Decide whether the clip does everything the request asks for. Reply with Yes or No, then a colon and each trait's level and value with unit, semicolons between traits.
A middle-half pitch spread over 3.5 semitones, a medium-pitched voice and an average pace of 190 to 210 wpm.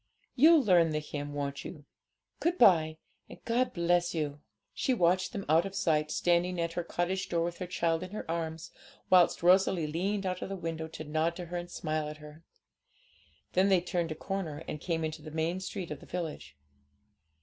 No: average, 2.8 semitones; medium, 170 Hz; average, 200 wpm